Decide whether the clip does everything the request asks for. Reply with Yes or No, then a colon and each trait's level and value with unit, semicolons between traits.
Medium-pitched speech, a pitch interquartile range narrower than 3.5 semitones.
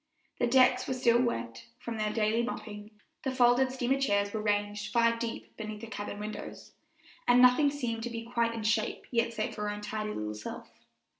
No: high, 230 Hz; narrow, 2.5 semitones